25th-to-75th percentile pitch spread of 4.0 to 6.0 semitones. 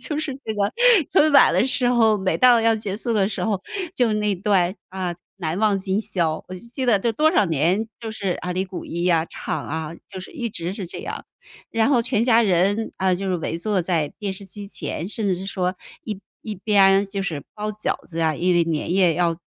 No: average, 3.6 semitones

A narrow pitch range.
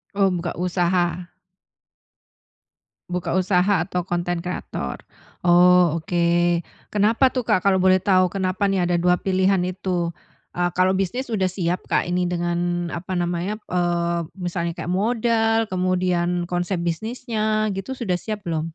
Yes: narrow, 2.0 semitones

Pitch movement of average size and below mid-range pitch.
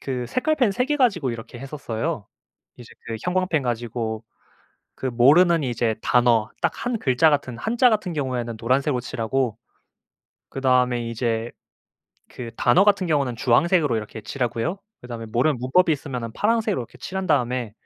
No: wide, 6.4 semitones; low, 130 Hz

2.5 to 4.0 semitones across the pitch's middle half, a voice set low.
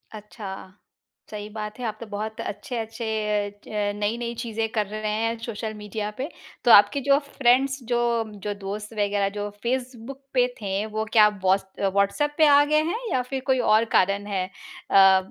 No: average, 3.1 semitones; high, 215 Hz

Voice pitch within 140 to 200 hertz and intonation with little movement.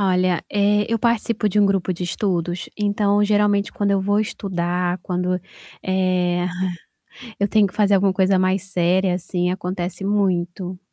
Yes: high, 190 Hz; narrow, 2.1 semitones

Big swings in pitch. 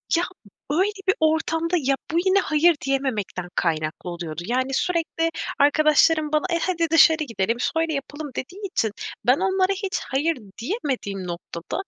Yes: wide, 5.7 semitones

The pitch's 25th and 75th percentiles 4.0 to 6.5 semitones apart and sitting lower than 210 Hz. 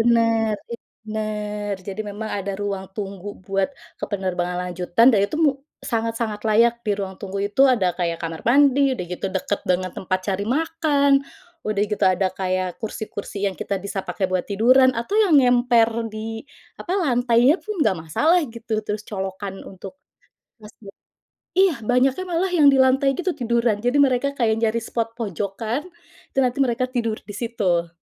No: average, 4.3 semitones; high, 220 Hz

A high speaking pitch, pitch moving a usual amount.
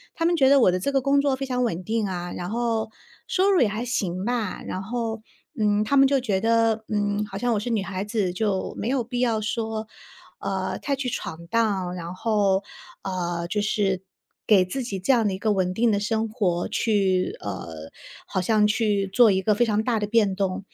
Yes: high, 210 Hz; average, 3.6 semitones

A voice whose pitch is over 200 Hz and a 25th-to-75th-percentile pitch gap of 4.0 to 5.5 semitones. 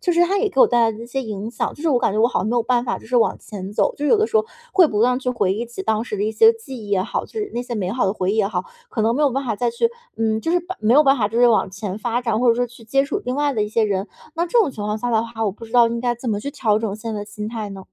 No: high, 235 Hz; average, 3.5 semitones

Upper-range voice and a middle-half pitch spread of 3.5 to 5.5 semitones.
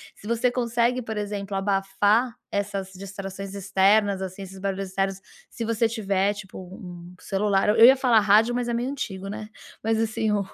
No: high, 205 Hz; narrow, 2.6 semitones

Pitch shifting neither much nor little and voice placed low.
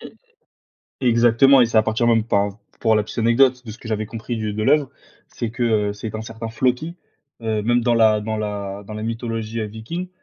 No: narrow, 1.9 semitones; low, 115 Hz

